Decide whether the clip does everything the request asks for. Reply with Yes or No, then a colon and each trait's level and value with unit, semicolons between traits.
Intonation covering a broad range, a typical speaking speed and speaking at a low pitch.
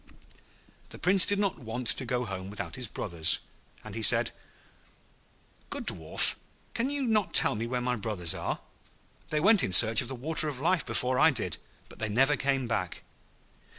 Yes: wide, 6.4 semitones; average, 185 wpm; low, 125 Hz